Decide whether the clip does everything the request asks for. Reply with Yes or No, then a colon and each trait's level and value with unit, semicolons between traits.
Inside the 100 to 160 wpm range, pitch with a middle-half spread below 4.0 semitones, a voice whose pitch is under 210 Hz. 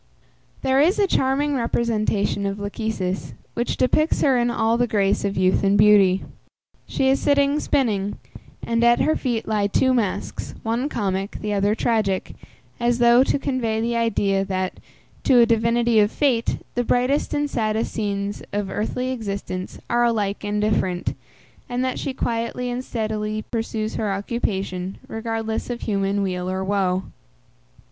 No: average, 155 wpm; average, 3.4 semitones; high, 220 Hz